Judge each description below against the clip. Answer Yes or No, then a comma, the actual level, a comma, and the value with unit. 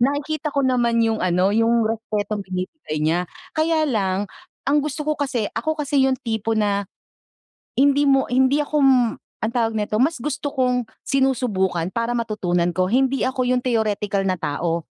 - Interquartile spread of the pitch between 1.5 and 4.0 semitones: No, average, 5.2 semitones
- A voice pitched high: Yes, high, 235 Hz